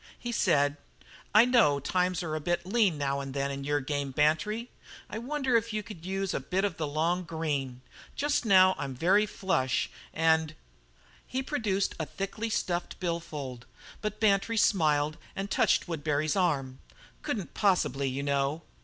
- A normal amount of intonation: No, wide, 5.9 semitones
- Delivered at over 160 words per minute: Yes, average, 170 wpm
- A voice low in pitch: No, medium, 170 Hz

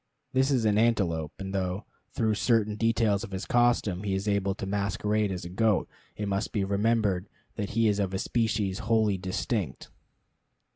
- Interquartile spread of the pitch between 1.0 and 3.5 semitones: Yes, narrow, 2.6 semitones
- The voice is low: Yes, low, 105 Hz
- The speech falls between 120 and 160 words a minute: No, average, 180 wpm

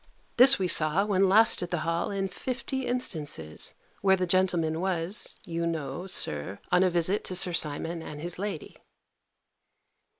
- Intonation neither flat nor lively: Yes, average, 3.1 semitones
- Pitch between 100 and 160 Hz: No, medium, 175 Hz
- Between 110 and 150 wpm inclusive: No, average, 160 wpm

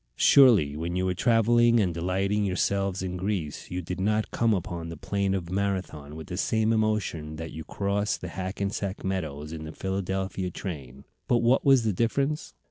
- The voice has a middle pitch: No, very low, 95 Hz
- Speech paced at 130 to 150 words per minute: No, average, 180 wpm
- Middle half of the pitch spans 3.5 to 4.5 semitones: Yes, average, 3.8 semitones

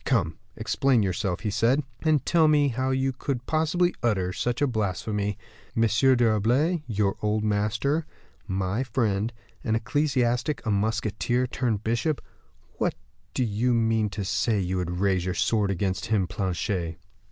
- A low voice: Yes, low, 110 Hz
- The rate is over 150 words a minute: No, average, 145 wpm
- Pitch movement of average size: Yes, average, 4.4 semitones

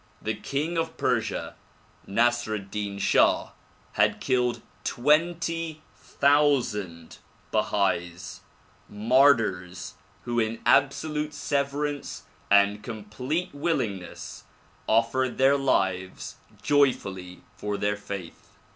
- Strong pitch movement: Yes, wide, 5.9 semitones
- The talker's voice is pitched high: No, low, 120 Hz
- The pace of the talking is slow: Yes, slow, 95 wpm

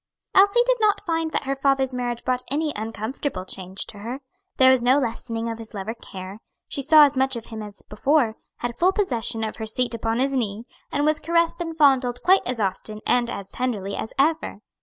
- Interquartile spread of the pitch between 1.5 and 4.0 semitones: No, average, 4.6 semitones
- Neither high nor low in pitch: No, very high, 250 Hz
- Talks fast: Yes, fast, 215 wpm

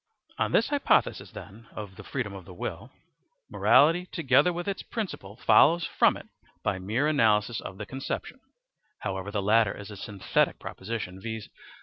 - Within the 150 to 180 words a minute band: Yes, average, 155 wpm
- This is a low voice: Yes, low, 110 Hz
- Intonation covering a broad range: Yes, wide, 6.3 semitones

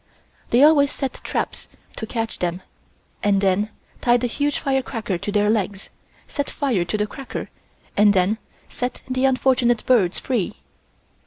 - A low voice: No, high, 225 Hz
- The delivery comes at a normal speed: Yes, average, 155 wpm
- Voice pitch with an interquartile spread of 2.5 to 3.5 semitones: No, average, 4.3 semitones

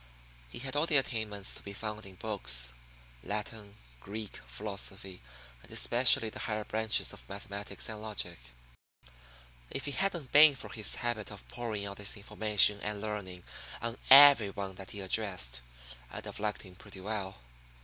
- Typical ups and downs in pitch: No, narrow, 2.3 semitones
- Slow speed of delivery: No, average, 160 wpm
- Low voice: Yes, low, 105 Hz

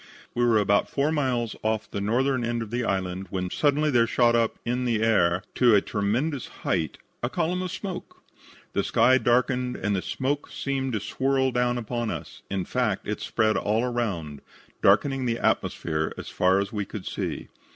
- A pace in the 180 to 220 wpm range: Yes, average, 185 wpm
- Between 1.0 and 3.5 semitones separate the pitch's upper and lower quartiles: No, average, 4.1 semitones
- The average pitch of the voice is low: Yes, low, 120 Hz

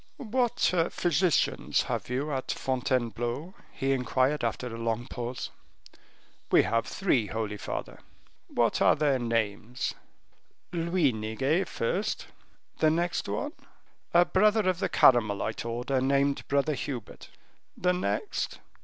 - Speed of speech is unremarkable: No, slow, 120 wpm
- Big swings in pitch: Yes, wide, 6.5 semitones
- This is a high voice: No, low, 135 Hz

